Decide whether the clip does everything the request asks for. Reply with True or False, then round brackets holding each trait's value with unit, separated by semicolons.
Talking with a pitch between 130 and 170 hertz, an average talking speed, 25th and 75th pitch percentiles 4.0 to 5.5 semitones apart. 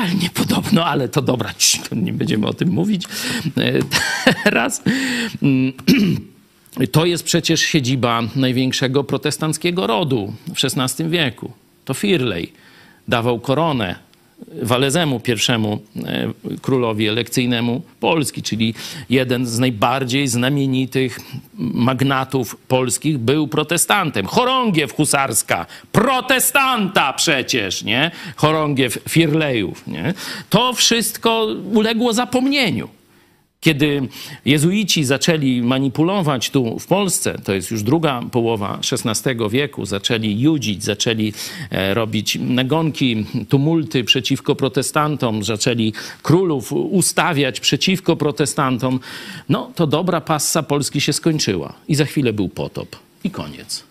False (140 Hz; 100 wpm; 5.2 semitones)